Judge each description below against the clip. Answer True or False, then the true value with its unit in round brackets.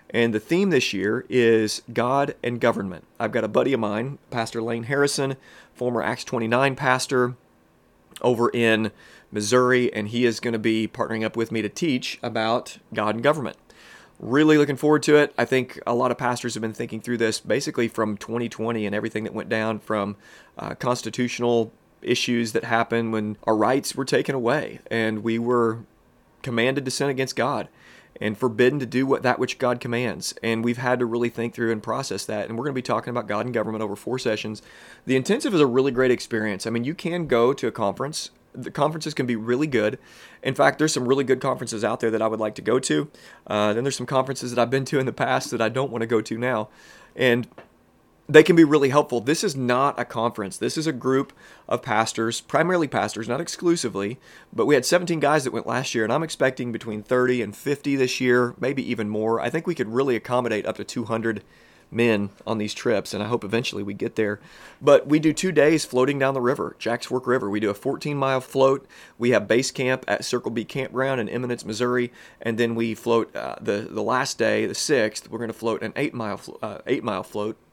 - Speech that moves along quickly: True (220 wpm)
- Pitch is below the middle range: True (120 Hz)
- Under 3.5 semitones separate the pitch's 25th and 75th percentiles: True (2.9 semitones)